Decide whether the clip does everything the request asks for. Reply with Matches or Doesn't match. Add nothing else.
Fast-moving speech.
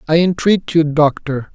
Doesn't match